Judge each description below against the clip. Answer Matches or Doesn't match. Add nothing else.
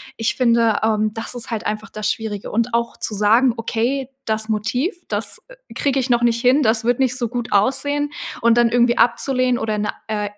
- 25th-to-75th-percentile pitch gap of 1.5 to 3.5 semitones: Matches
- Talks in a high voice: Matches